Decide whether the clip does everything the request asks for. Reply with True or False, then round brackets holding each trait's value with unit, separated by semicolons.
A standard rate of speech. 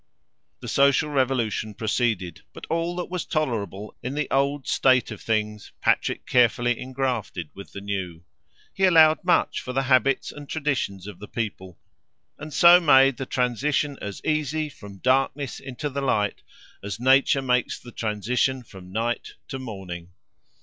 True (155 wpm)